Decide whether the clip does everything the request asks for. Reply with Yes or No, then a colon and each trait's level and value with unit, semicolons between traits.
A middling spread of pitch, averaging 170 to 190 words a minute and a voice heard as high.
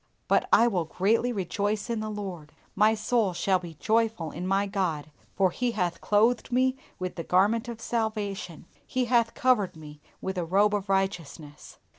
Yes: average, 4.0 semitones; average, 175 wpm; high, 200 Hz